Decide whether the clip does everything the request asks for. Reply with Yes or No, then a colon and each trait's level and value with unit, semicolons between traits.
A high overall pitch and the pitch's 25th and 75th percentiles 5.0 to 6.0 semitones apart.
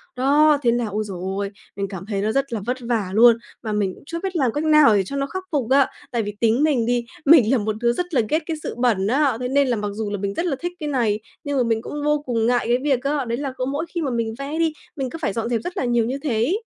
No: high, 245 Hz; average, 4.6 semitones